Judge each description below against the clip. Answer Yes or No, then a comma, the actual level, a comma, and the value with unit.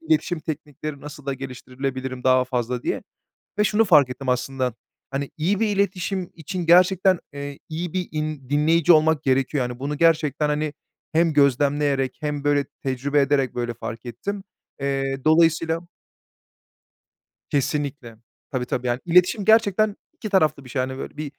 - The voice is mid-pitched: Yes, medium, 145 Hz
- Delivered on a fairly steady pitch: No, average, 3.9 semitones